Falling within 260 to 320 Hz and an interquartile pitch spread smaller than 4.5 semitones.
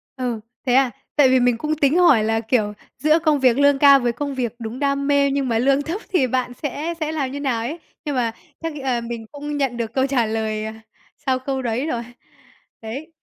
Yes: very high, 265 Hz; average, 3.3 semitones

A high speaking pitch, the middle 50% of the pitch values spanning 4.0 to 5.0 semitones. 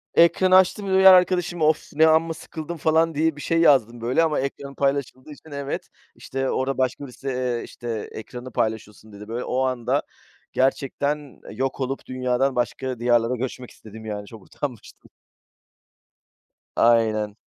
No: low, 130 Hz; average, 4.6 semitones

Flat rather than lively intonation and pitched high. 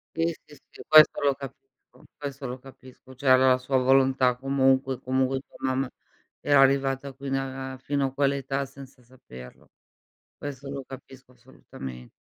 No: narrow, 1.0 semitones; low, 135 Hz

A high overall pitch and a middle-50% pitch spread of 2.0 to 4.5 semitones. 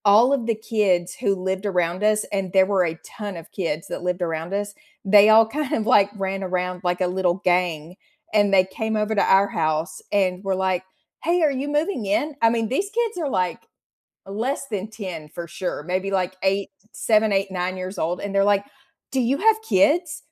Yes: high, 195 Hz; average, 3.3 semitones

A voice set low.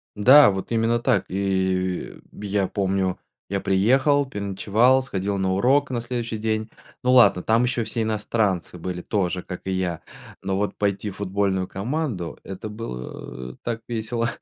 Yes: low, 100 Hz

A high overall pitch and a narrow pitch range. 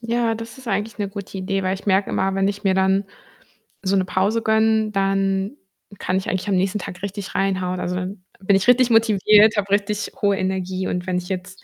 Yes: high, 195 Hz; narrow, 2.0 semitones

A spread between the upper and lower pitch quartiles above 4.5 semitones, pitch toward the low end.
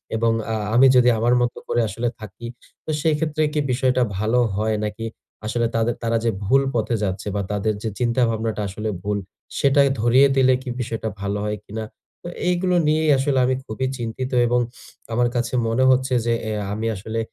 No: average, 2.9 semitones; low, 120 Hz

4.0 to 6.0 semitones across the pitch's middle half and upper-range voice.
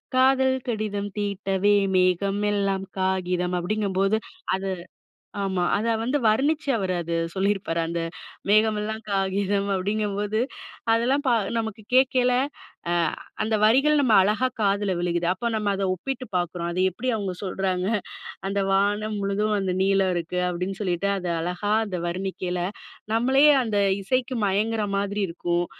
No: narrow, 2.6 semitones; high, 200 Hz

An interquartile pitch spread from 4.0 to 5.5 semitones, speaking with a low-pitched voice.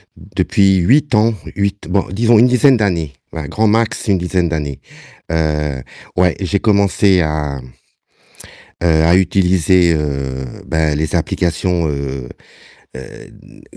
Yes: average, 4.7 semitones; very low, 90 Hz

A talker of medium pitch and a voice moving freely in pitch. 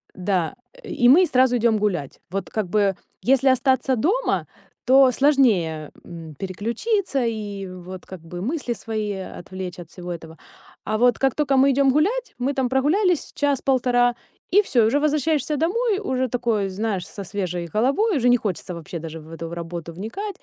No: high, 235 Hz; wide, 6.8 semitones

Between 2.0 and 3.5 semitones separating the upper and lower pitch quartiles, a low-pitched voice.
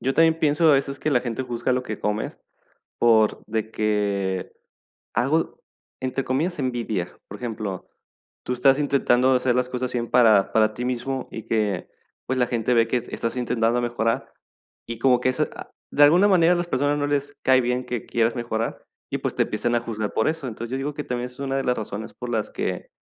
Yes: average, 3.1 semitones; low, 125 Hz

